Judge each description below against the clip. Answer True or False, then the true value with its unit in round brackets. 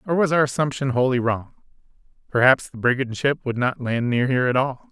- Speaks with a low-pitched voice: True (130 Hz)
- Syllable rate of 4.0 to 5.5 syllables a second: False (5.8 syllables/s)